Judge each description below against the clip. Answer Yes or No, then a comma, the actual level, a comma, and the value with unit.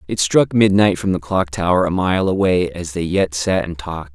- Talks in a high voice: No, very low, 90 Hz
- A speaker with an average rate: No, fast, 230 wpm